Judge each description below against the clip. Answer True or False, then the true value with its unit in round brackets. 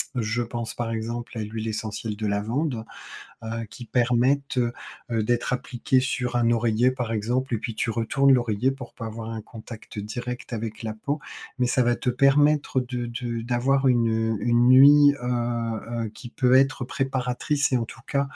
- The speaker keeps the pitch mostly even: True (2.3 semitones)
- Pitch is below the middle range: True (120 Hz)